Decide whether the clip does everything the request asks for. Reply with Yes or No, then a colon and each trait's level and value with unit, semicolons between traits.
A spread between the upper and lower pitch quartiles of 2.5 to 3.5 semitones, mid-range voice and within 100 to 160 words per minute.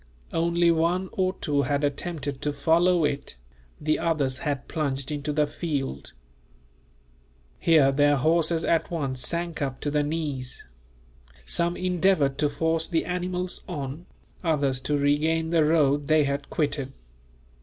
Yes: average, 2.9 semitones; medium, 150 Hz; average, 140 wpm